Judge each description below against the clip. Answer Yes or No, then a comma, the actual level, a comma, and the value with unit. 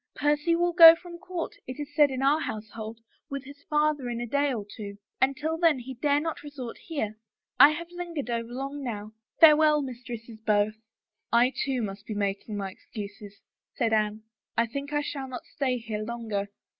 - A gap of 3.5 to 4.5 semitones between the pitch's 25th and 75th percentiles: No, average, 5.2 semitones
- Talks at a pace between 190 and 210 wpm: Yes, average, 200 wpm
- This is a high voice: Yes, very high, 255 Hz